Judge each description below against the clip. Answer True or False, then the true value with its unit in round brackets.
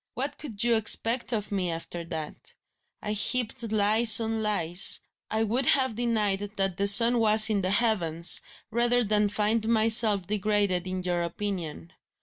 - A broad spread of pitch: False (2.9 semitones)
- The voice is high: True (210 Hz)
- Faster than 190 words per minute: False (155 wpm)